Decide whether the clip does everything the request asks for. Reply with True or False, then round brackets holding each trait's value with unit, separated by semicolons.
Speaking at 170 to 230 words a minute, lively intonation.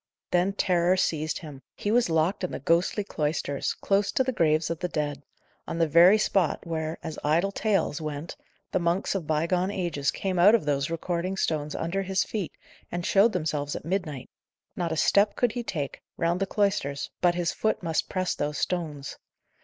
False (190 wpm; 3.8 semitones)